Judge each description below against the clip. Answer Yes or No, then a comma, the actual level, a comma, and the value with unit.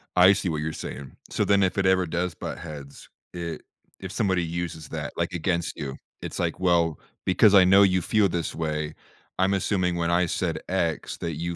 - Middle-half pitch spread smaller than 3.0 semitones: Yes, narrow, 2.6 semitones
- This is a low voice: Yes, very low, 85 Hz